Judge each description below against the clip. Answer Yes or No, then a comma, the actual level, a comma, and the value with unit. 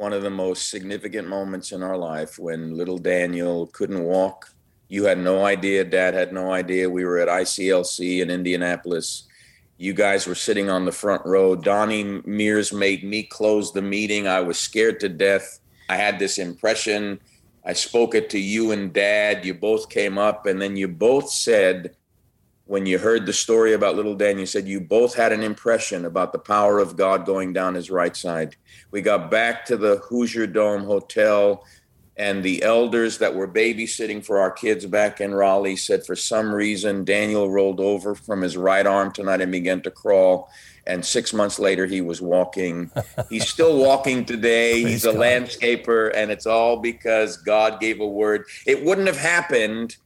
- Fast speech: No, average, 185 wpm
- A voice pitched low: Yes, low, 100 Hz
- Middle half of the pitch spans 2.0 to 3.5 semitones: Yes, average, 2.7 semitones